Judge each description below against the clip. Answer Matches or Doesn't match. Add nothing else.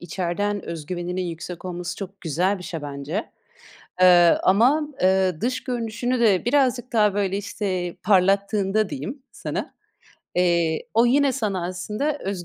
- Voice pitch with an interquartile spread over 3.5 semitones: Matches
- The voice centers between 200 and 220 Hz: Doesn't match